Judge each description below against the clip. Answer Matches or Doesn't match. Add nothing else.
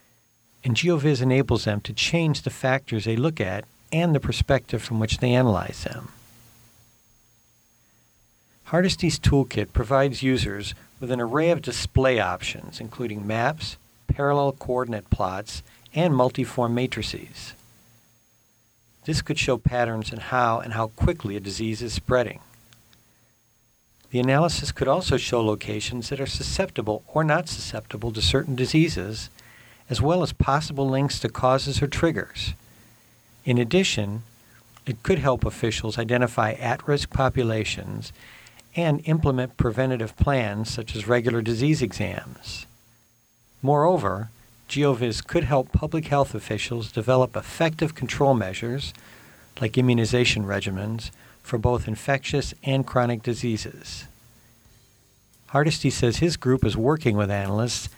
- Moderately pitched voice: Doesn't match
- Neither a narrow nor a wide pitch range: Matches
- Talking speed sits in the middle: Doesn't match